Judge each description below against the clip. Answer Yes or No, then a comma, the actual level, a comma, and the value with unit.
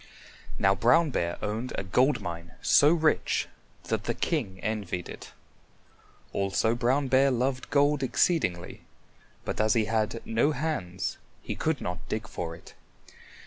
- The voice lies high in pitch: No, low, 115 Hz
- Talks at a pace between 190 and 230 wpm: No, average, 145 wpm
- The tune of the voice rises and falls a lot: Yes, wide, 6.5 semitones